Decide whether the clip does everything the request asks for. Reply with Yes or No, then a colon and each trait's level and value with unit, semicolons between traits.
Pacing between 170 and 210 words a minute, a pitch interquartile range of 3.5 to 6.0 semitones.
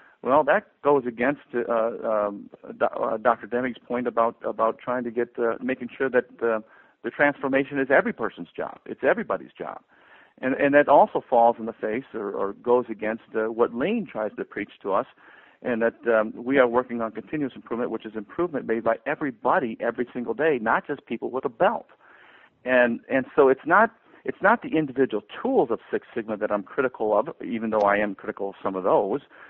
No: average, 200 wpm; average, 2.9 semitones